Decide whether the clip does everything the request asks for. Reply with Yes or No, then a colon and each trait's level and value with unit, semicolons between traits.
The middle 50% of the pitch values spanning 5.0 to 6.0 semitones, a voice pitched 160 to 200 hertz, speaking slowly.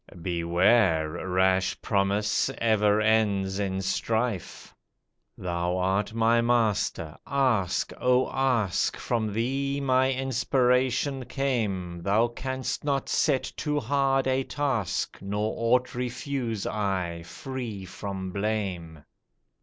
No: average, 5.3 semitones; low, 110 Hz; slow, 105 wpm